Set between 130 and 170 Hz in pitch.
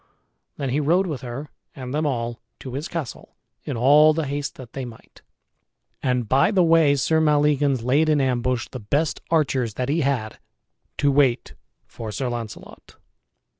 Yes: medium, 140 Hz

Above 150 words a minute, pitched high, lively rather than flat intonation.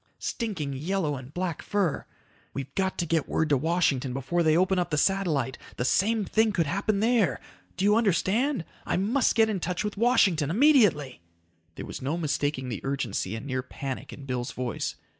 No: average, 185 wpm; medium, 170 Hz; wide, 6.5 semitones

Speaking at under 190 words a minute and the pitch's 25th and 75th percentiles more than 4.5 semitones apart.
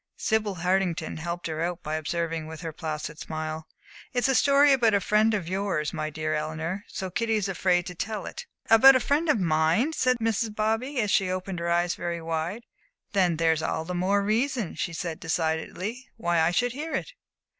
No: average, 200 wpm; average, 5.3 semitones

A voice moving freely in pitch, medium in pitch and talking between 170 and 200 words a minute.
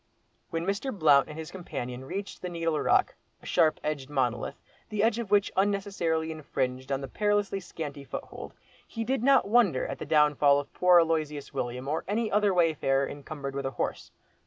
Yes: wide, 6.2 semitones; medium, 160 Hz; average, 185 wpm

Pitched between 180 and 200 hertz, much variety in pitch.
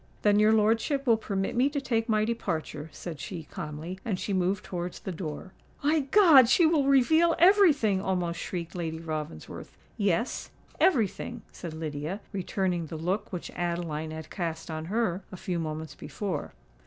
Yes: high, 190 Hz; wide, 5.9 semitones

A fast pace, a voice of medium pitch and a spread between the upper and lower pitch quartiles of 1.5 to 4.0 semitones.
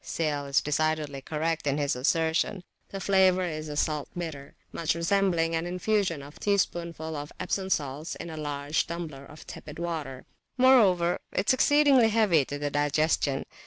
No: average, 165 wpm; medium, 160 Hz; average, 3.7 semitones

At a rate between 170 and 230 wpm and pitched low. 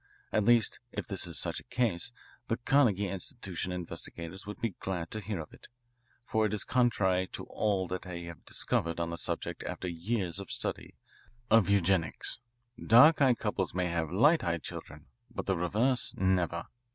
Yes: average, 175 wpm; very low, 95 Hz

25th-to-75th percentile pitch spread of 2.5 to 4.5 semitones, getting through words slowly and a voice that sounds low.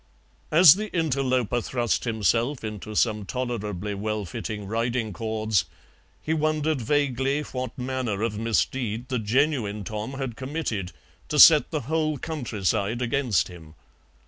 Yes: average, 4.1 semitones; slow, 130 wpm; low, 120 Hz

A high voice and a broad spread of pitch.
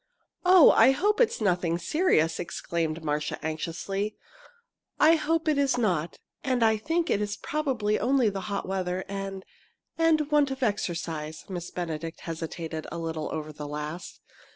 Yes: high, 195 Hz; wide, 8.6 semitones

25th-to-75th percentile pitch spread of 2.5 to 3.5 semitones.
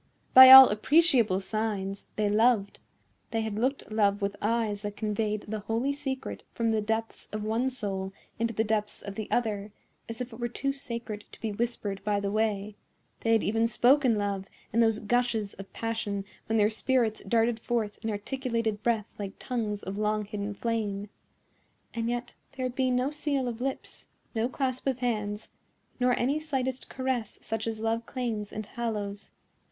Yes: average, 2.8 semitones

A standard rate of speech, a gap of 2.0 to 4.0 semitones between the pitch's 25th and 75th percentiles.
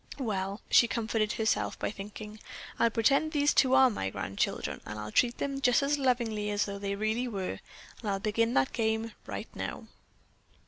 Yes: average, 180 wpm; average, 3.4 semitones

